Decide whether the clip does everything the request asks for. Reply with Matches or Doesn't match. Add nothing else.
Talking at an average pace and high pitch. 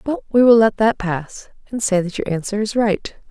Doesn't match